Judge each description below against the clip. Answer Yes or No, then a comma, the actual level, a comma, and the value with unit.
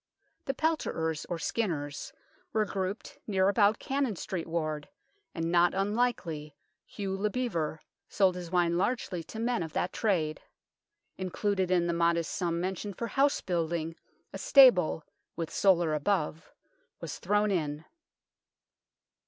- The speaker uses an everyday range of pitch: Yes, average, 3.9 semitones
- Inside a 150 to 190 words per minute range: No, slow, 135 wpm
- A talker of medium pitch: Yes, medium, 180 Hz